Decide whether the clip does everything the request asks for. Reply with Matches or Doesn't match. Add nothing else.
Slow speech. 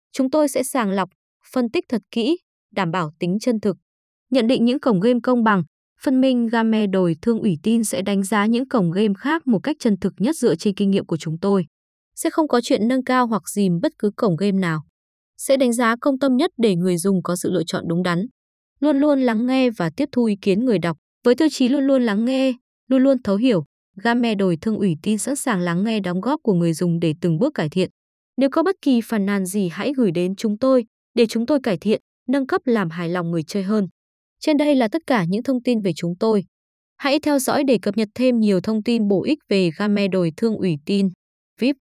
Doesn't match